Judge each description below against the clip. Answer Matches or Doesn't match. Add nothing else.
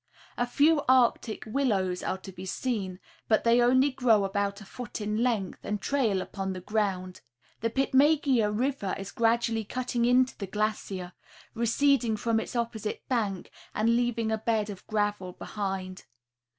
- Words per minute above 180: Doesn't match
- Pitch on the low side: Doesn't match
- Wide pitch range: Doesn't match